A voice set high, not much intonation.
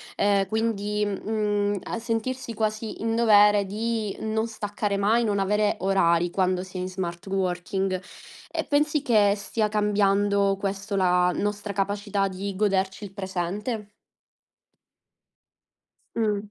Yes: high, 205 Hz; narrow, 1.8 semitones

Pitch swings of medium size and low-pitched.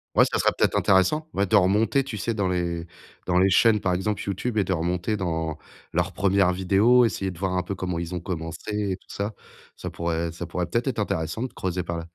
Yes: average, 3.0 semitones; very low, 95 Hz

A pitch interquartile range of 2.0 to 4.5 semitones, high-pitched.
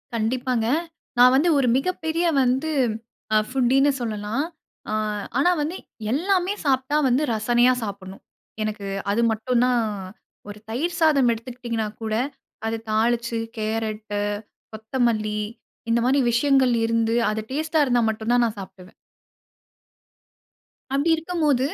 Yes: average, 3.8 semitones; high, 240 Hz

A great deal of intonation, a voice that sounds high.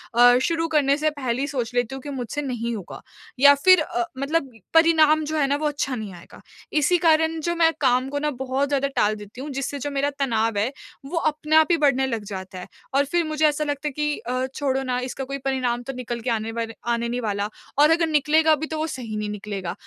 No: average, 4.1 semitones; very high, 275 Hz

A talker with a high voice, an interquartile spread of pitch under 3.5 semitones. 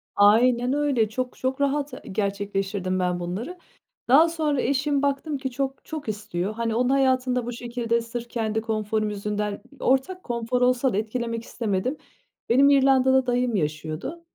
No: high, 240 Hz; average, 4.1 semitones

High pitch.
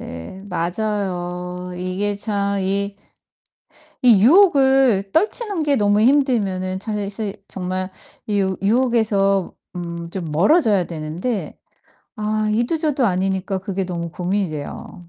Yes: high, 200 Hz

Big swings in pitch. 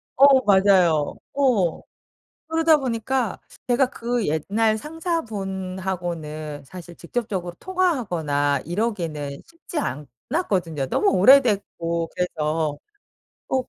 Yes: wide, 7.2 semitones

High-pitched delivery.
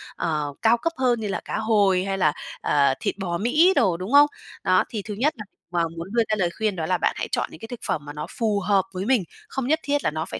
Yes: high, 200 Hz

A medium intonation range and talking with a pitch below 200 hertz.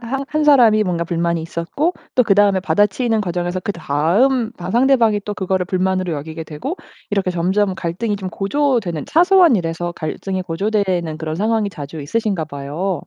Yes: average, 4.8 semitones; high, 190 Hz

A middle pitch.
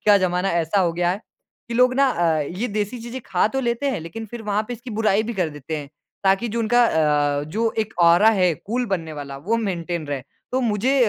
No: high, 200 Hz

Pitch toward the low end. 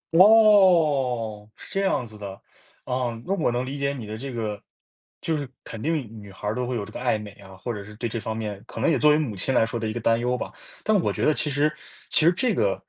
Yes: low, 125 Hz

